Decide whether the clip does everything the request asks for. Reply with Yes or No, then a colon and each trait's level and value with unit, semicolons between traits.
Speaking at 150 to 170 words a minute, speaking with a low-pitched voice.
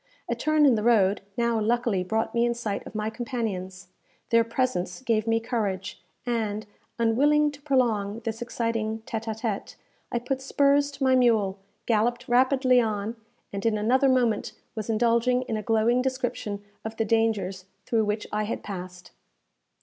No: average, 165 wpm; high, 225 Hz